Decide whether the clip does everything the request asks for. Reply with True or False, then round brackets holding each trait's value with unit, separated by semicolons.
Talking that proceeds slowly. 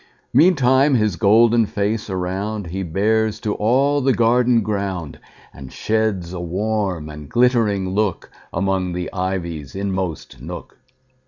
True (110 wpm)